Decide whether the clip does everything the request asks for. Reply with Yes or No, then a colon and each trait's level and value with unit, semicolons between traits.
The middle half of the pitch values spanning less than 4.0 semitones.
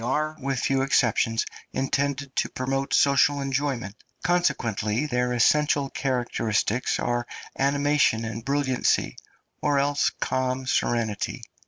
Yes: average, 2.8 semitones